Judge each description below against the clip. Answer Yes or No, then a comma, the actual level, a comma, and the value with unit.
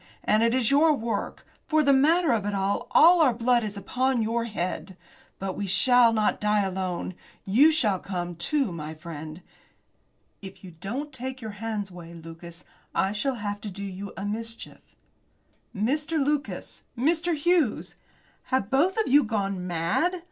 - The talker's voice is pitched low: No, high, 215 Hz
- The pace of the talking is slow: No, average, 165 wpm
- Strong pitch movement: Yes, wide, 6.0 semitones